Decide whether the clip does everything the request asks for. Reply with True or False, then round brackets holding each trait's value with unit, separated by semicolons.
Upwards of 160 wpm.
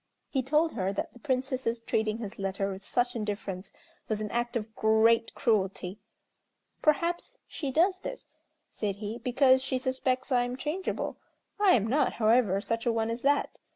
True (170 wpm)